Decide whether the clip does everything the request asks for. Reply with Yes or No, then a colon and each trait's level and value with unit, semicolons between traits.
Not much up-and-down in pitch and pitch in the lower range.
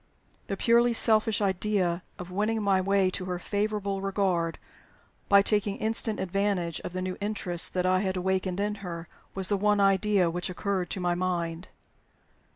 No: narrow, 2.3 semitones; high, 195 Hz